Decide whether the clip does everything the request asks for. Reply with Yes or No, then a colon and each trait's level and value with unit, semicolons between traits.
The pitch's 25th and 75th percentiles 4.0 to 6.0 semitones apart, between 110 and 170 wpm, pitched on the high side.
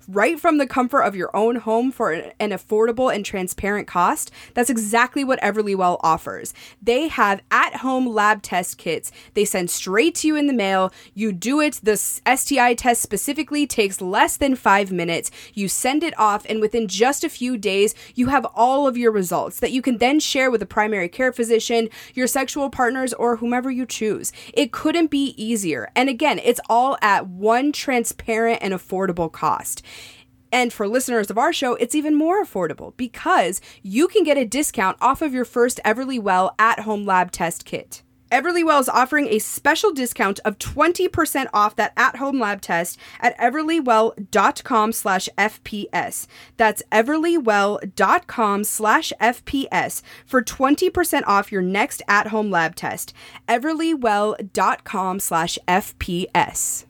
Yes: average, 4.5 semitones; average, 160 wpm; high, 230 Hz